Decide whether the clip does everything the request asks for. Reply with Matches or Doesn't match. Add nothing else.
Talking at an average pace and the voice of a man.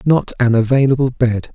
Matches